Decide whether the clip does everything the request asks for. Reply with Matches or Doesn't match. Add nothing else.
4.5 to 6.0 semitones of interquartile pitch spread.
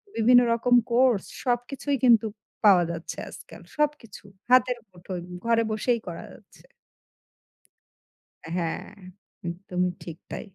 Matches